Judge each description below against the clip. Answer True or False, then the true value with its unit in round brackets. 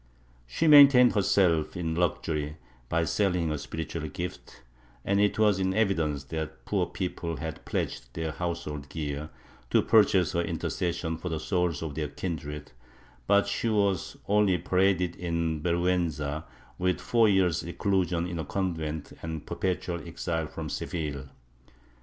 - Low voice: True (85 Hz)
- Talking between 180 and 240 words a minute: False (140 wpm)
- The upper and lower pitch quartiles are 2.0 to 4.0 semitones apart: True (3.1 semitones)